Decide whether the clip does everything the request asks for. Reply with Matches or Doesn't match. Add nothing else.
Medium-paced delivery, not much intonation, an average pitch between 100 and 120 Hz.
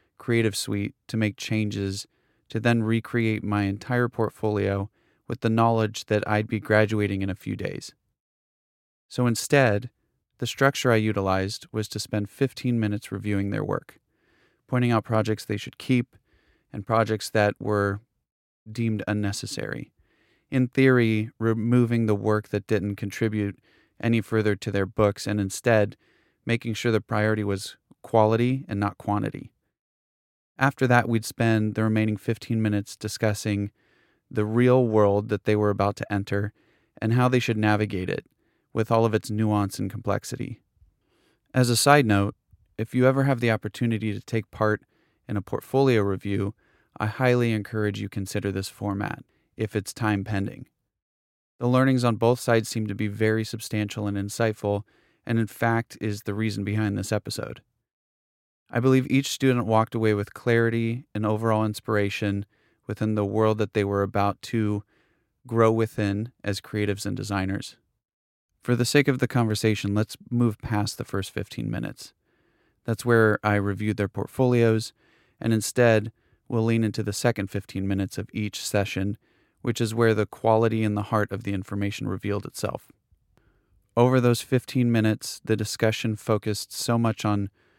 Matches